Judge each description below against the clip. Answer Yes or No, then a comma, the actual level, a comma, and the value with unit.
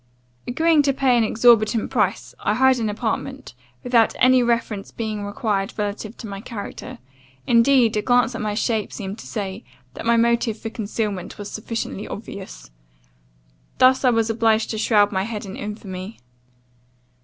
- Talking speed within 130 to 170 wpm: Yes, average, 160 wpm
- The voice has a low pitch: No, high, 225 Hz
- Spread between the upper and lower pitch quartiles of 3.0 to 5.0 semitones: No, narrow, 2.6 semitones